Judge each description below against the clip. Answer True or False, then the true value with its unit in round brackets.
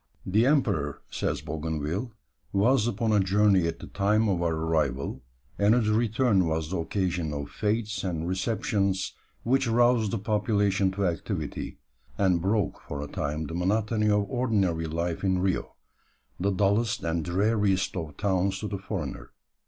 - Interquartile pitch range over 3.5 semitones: True (4.1 semitones)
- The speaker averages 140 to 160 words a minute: True (155 wpm)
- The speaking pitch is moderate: False (95 Hz)